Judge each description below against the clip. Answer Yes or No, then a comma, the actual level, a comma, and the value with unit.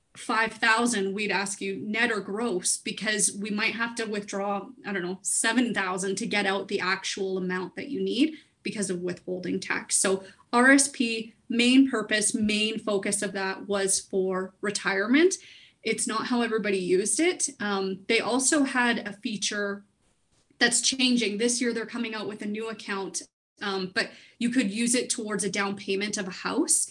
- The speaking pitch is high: Yes, high, 210 Hz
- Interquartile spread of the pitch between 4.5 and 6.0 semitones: No, average, 3.2 semitones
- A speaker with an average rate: Yes, average, 170 wpm